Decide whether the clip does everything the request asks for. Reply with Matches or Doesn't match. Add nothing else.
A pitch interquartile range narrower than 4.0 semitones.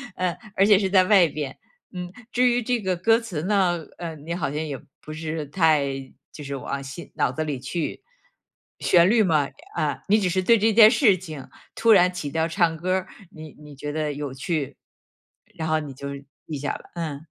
Doesn't match